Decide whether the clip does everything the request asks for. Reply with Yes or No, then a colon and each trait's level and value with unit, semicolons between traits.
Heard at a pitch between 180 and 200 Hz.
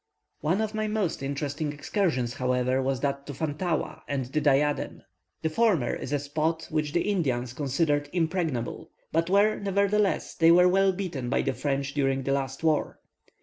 No: medium, 150 Hz